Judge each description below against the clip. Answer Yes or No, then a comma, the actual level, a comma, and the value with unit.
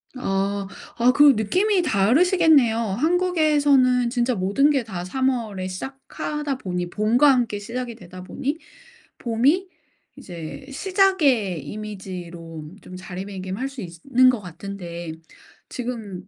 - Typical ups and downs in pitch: No, wide, 6.4 semitones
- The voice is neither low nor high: No, high, 230 Hz